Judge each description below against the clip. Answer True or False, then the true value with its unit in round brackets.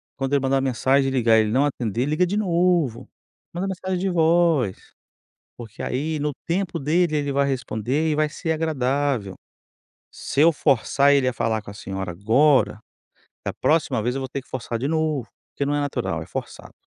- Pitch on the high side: False (140 Hz)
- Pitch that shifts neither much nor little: True (4.3 semitones)